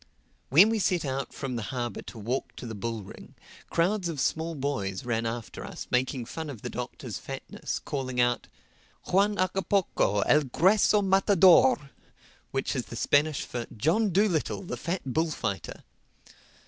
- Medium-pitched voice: Yes, medium, 145 Hz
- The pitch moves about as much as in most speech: No, wide, 7.2 semitones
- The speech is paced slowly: No, average, 155 wpm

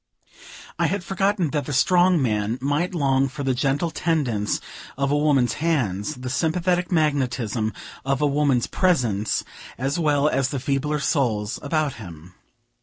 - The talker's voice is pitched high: No, medium, 140 Hz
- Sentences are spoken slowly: No, average, 150 wpm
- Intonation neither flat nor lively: Yes, average, 4.0 semitones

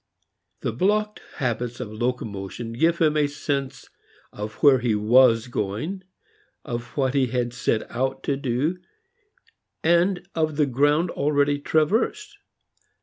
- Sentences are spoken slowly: Yes, slow, 130 wpm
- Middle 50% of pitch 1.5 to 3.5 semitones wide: No, average, 4.6 semitones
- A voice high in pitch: No, low, 135 Hz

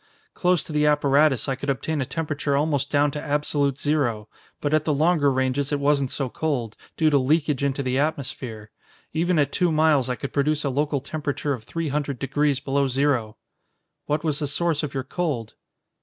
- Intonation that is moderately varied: No, narrow, 2.1 semitones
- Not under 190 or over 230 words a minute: Yes, average, 195 wpm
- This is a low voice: No, medium, 145 Hz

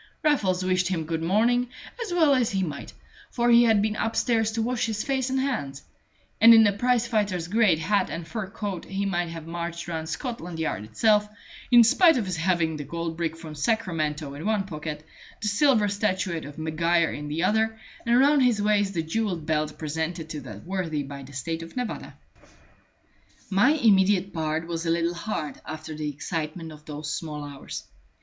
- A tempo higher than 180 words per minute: Yes, average, 190 wpm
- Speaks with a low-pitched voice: No, medium, 180 Hz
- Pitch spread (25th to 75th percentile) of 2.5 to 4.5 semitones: No, wide, 5.6 semitones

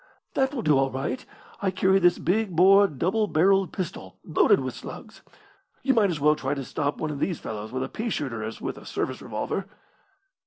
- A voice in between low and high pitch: Yes, medium, 175 Hz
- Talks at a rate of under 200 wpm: No, fast, 205 wpm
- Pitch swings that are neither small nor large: No, wide, 6.1 semitones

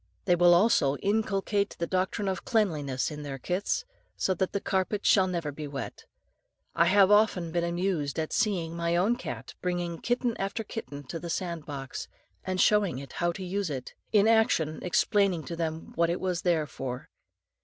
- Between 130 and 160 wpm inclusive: No, average, 185 wpm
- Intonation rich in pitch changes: No, average, 3.8 semitones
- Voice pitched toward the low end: No, medium, 175 Hz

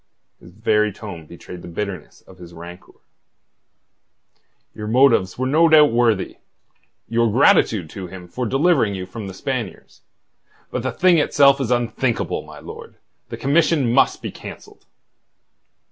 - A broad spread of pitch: Yes, wide, 6.1 semitones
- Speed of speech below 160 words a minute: Yes, average, 145 wpm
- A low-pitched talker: Yes, low, 115 Hz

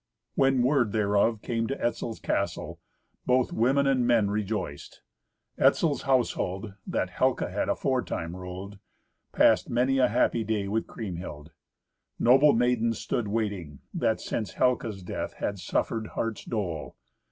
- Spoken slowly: Yes, slow, 130 wpm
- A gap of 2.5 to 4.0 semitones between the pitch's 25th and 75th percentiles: Yes, average, 3.7 semitones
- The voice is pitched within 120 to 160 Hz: No, low, 110 Hz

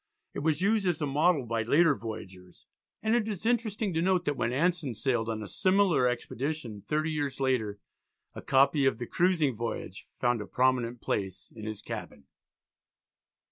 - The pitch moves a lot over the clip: Yes, wide, 6.9 semitones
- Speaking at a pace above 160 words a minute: Yes, average, 175 wpm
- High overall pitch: No, low, 135 Hz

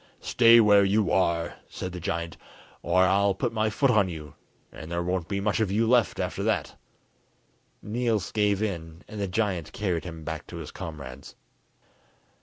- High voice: No, very low, 95 Hz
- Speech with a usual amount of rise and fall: Yes, average, 4.1 semitones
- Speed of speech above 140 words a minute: Yes, average, 175 wpm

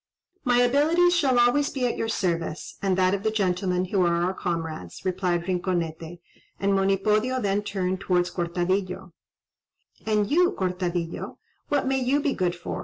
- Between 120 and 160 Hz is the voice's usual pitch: No, high, 190 Hz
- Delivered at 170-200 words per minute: No, average, 160 wpm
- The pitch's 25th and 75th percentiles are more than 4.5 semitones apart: Yes, wide, 5.4 semitones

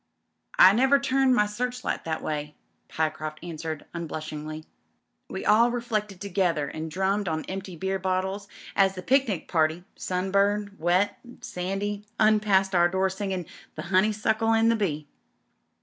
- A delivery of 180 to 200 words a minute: No, average, 140 wpm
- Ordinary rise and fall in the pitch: Yes, average, 3.9 semitones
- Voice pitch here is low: No, high, 190 Hz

